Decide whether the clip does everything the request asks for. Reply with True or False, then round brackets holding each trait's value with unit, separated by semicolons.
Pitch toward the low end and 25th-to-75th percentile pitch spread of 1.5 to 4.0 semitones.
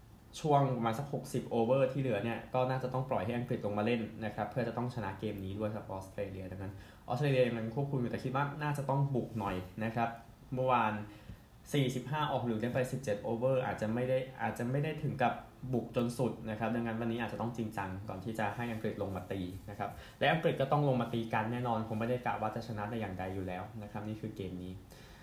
True (115 Hz; 3.4 semitones)